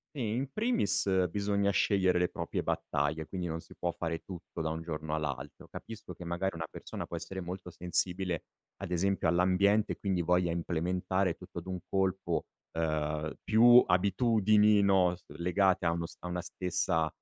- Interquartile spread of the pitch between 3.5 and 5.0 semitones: No, average, 2.7 semitones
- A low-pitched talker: Yes, very low, 90 Hz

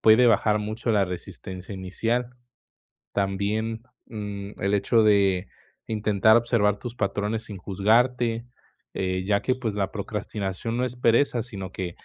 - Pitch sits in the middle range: No, low, 105 Hz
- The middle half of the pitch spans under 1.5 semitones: No, average, 2.7 semitones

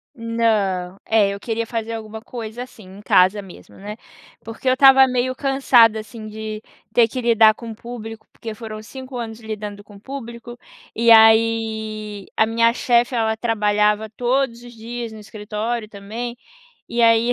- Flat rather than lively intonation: Yes, narrow, 1.8 semitones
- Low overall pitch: No, high, 225 Hz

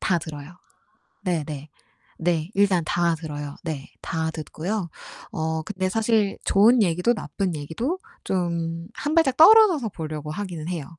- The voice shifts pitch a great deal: No, average, 4.7 semitones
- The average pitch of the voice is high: No, medium, 175 Hz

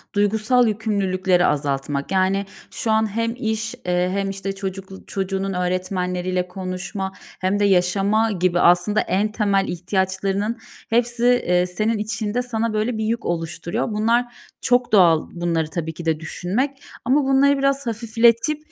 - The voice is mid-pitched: No, high, 195 Hz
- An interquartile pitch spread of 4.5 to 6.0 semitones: No, average, 3.8 semitones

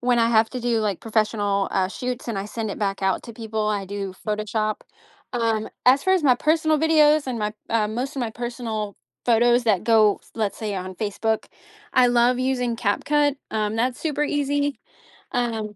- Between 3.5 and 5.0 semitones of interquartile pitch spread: No, average, 3.1 semitones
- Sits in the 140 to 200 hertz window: No, high, 230 Hz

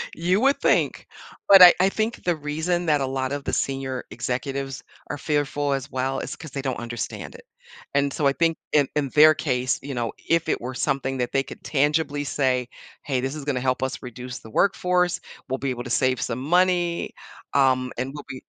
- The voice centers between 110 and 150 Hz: Yes, medium, 140 Hz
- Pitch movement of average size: Yes, average, 3.3 semitones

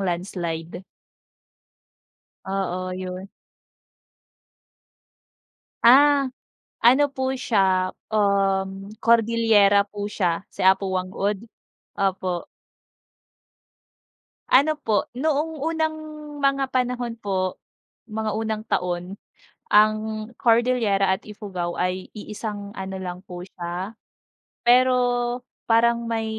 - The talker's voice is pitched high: Yes, high, 205 Hz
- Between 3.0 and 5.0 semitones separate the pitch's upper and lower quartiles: Yes, average, 3.8 semitones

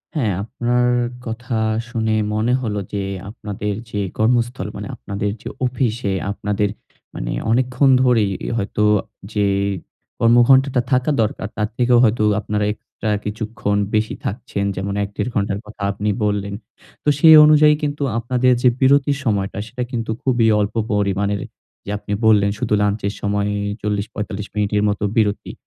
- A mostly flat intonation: No, average, 3.1 semitones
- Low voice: Yes, low, 110 Hz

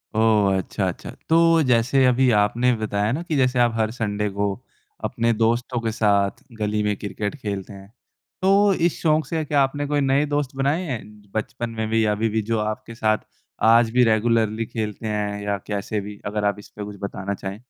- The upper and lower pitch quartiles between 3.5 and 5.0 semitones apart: Yes, average, 3.8 semitones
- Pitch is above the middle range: No, low, 110 Hz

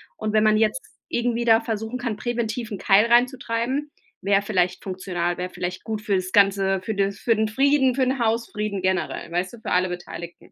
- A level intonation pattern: No, average, 3.9 semitones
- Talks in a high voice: Yes, high, 215 Hz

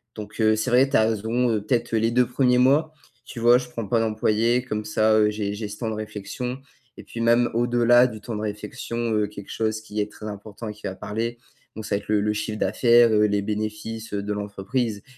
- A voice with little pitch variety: Yes, narrow, 2.1 semitones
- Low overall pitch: Yes, low, 110 Hz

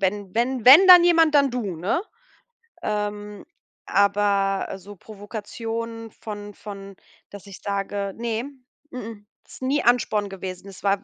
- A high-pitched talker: Yes, high, 205 Hz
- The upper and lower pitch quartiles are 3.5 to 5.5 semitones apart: No, average, 2.8 semitones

